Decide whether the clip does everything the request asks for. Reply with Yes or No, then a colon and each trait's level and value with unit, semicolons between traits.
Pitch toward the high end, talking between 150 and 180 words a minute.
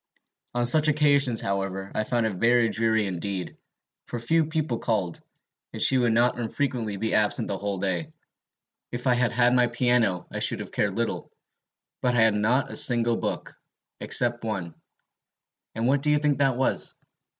No: low, 120 Hz; average, 175 wpm